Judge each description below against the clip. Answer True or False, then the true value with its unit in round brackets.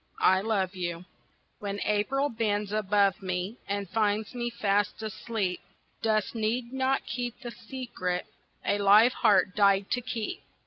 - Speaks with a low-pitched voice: False (210 Hz)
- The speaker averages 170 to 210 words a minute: False (140 wpm)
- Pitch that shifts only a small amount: False (3.0 semitones)